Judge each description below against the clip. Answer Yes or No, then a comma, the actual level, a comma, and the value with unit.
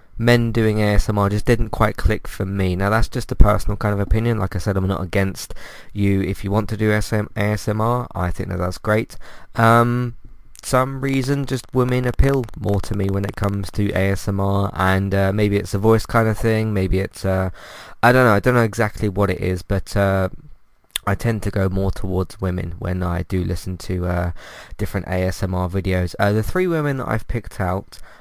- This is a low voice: Yes, low, 100 Hz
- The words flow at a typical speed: No, fast, 210 wpm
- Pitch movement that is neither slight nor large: Yes, average, 3.1 semitones